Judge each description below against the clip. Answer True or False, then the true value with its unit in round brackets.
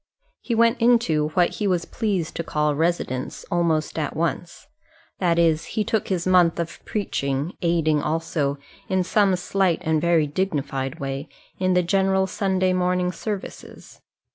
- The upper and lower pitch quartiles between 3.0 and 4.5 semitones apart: True (3.3 semitones)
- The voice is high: False (175 Hz)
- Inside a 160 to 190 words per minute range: False (150 wpm)